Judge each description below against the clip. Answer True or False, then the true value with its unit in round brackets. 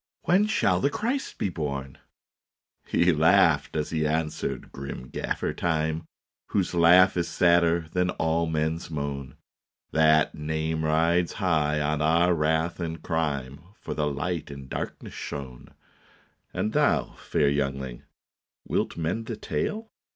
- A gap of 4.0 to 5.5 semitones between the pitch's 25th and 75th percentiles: False (2.6 semitones)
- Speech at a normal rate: True (145 wpm)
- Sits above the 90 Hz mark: False (80 Hz)